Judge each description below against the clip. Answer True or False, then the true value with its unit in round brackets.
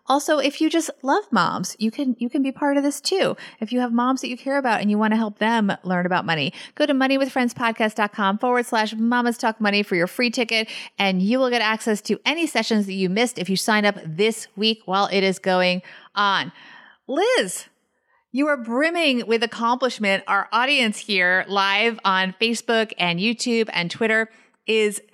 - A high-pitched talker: True (225 Hz)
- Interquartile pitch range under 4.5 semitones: True (4.1 semitones)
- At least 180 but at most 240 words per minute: True (200 wpm)